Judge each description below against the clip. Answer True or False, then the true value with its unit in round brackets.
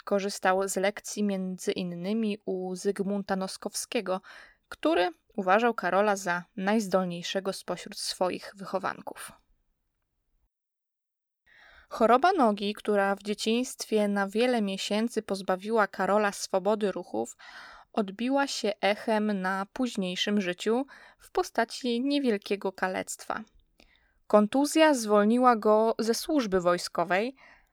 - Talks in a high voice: True (210 Hz)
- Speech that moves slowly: True (95 wpm)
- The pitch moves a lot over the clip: False (3.4 semitones)